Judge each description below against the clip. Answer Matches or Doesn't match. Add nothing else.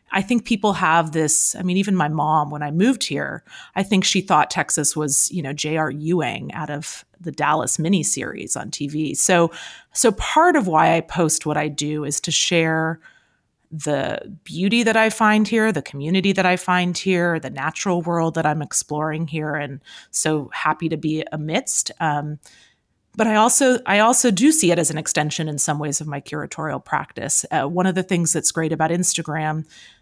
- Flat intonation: Doesn't match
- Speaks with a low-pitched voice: Doesn't match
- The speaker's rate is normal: Matches